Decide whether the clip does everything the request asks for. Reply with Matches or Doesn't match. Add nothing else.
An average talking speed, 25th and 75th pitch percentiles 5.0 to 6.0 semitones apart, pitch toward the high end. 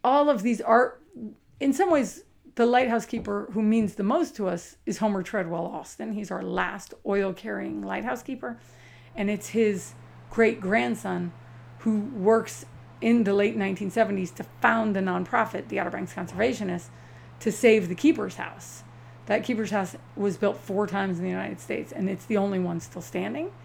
Doesn't match